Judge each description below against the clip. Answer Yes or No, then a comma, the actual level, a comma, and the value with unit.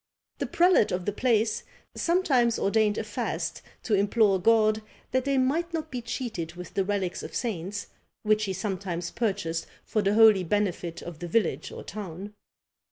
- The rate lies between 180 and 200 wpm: No, average, 165 wpm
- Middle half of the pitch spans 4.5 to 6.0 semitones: No, average, 3.8 semitones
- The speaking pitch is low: No, high, 210 Hz